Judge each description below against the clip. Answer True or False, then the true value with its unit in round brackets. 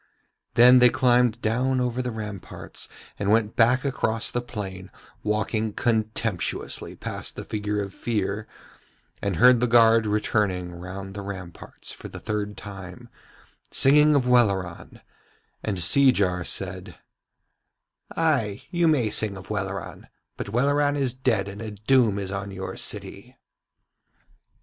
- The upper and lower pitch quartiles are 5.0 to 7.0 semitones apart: False (3.9 semitones)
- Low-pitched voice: True (110 Hz)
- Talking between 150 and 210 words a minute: False (135 wpm)